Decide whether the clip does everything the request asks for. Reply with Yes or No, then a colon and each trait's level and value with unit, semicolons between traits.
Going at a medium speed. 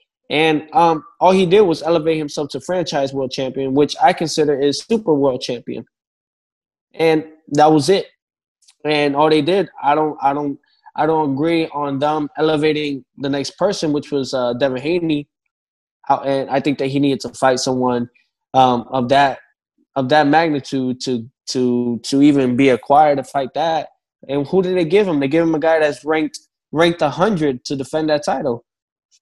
Yes: average, 180 wpm